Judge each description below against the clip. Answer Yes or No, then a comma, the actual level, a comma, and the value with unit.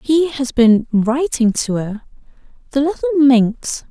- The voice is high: Yes, very high, 265 Hz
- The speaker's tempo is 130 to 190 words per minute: Yes, average, 140 wpm